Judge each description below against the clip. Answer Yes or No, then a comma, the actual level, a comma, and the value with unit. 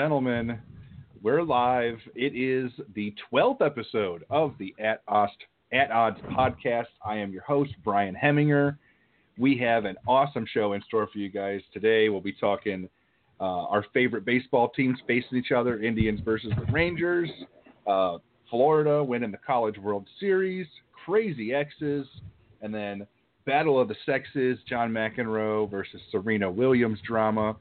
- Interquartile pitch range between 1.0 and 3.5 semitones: No, average, 4.1 semitones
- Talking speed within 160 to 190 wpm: No, average, 150 wpm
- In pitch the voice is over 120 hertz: No, low, 115 Hz